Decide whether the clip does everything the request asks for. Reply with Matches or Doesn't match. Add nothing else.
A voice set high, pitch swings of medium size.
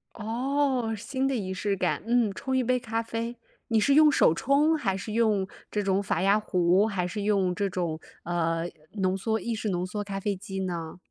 Matches